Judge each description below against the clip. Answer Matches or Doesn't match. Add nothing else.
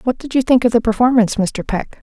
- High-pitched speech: Matches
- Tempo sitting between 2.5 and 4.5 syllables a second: Doesn't match